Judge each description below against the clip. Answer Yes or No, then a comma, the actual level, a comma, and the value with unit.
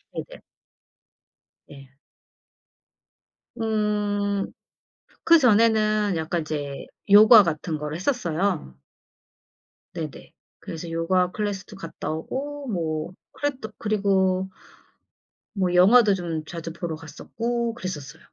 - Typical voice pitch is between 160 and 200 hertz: Yes, high, 190 Hz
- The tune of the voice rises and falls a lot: No, average, 4.7 semitones